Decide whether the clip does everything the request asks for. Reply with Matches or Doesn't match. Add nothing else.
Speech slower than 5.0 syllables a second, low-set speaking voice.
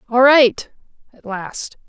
Doesn't match